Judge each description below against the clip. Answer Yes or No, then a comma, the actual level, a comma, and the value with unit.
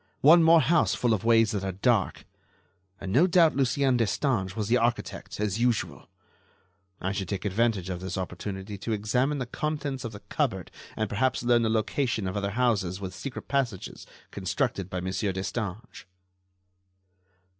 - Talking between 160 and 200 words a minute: Yes, average, 165 wpm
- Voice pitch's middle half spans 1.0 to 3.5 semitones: No, average, 4.7 semitones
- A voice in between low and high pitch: No, low, 110 Hz